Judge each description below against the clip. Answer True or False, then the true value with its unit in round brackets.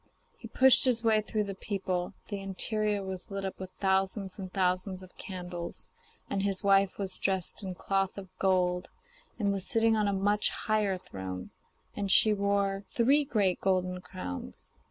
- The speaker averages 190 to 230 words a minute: False (170 wpm)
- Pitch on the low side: False (195 Hz)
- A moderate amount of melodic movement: False (1.9 semitones)